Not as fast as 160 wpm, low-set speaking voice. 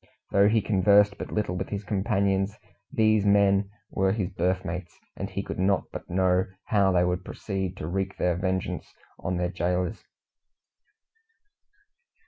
Yes: average, 150 wpm; very low, 95 Hz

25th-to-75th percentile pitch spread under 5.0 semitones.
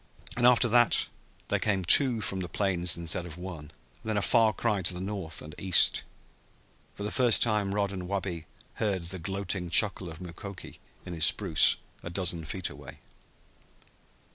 Yes: average, 3.2 semitones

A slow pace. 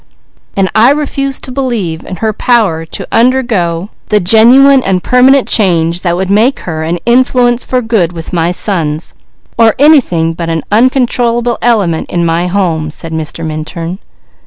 No: average, 160 wpm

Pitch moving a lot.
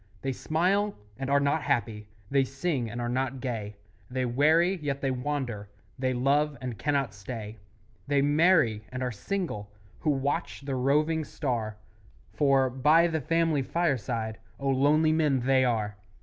No: average, 3.7 semitones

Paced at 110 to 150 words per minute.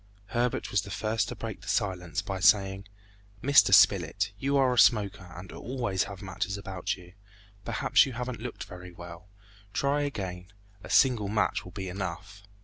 No: average, 165 wpm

